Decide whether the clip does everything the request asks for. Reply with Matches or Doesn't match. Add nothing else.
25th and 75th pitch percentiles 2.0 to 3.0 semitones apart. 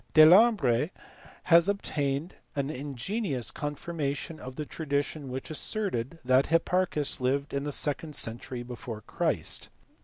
Doesn't match